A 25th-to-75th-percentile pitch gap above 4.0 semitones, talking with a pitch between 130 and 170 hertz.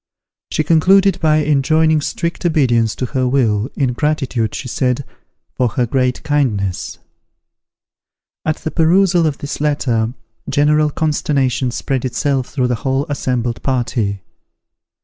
No: average, 3.7 semitones; low, 135 Hz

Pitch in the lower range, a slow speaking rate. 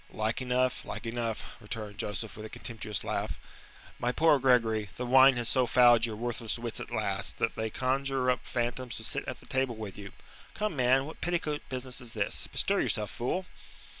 No: low, 120 Hz; average, 195 wpm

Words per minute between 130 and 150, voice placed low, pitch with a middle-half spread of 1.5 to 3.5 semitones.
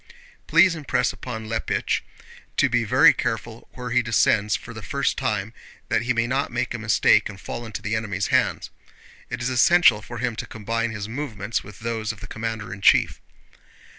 No: average, 190 wpm; low, 115 Hz; narrow, 2.5 semitones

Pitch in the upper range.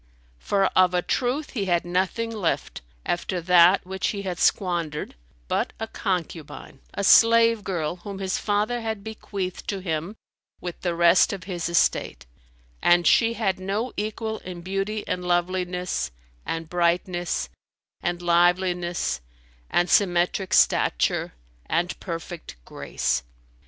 No: medium, 180 Hz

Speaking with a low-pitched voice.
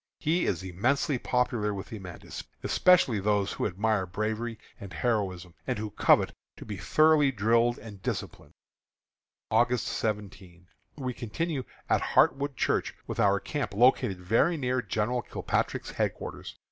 Yes: low, 110 Hz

